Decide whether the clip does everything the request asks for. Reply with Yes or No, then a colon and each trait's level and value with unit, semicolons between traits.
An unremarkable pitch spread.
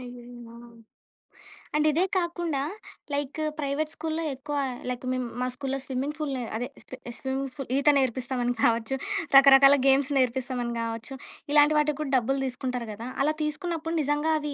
Yes: average, 3.1 semitones